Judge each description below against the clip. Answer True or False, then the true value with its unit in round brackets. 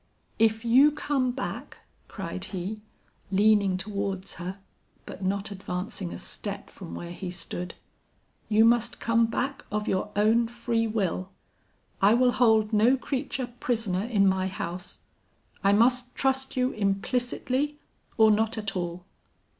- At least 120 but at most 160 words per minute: True (140 wpm)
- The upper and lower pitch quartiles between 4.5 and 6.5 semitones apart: False (3.8 semitones)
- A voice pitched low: False (215 Hz)